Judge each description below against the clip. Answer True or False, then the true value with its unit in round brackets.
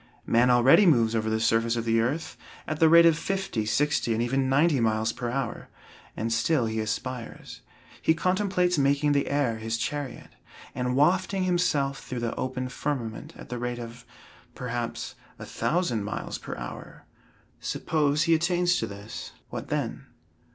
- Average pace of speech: True (165 wpm)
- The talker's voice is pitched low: True (130 Hz)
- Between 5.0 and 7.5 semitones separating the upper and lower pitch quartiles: True (5.3 semitones)